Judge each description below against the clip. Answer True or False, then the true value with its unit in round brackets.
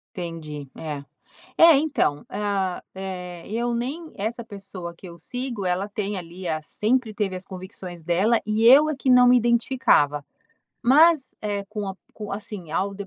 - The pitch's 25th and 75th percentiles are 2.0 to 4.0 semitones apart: False (5.1 semitones)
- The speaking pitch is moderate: False (200 Hz)